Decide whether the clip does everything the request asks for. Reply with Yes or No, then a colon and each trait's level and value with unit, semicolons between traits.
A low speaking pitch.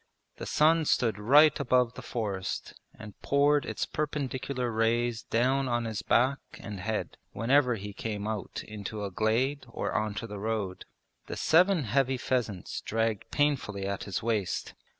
Yes: low, 115 Hz